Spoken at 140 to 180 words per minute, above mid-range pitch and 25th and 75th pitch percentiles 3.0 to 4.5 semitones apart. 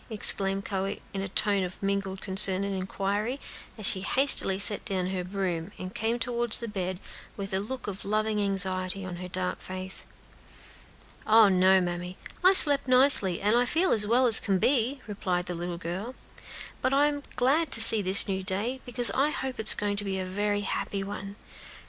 No: average, 190 wpm; high, 200 Hz; average, 3.3 semitones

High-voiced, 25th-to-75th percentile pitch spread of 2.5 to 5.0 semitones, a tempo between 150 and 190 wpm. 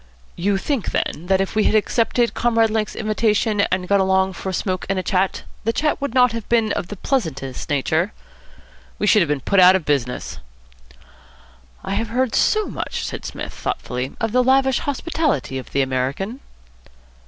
Yes: high, 205 Hz; average, 4.6 semitones; average, 185 wpm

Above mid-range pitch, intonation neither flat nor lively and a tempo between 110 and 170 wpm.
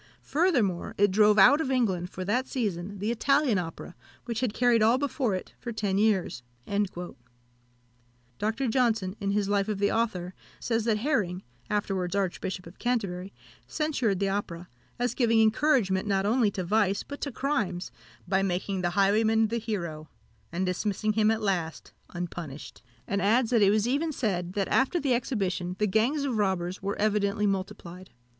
Yes: high, 205 Hz; average, 3.7 semitones; average, 165 wpm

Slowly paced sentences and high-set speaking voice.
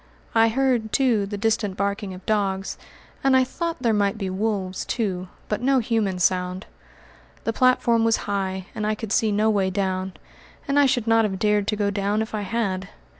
No: average, 195 wpm; high, 210 Hz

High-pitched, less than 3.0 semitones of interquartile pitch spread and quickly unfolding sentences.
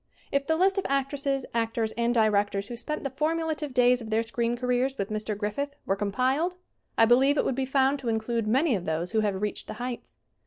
No: high, 245 Hz; average, 4.0 semitones; fast, 220 wpm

